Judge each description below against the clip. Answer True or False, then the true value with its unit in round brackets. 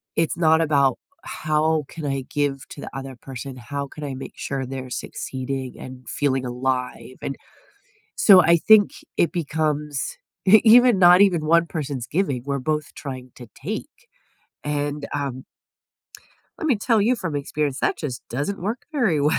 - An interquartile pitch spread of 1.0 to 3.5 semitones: False (4.1 semitones)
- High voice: False (145 Hz)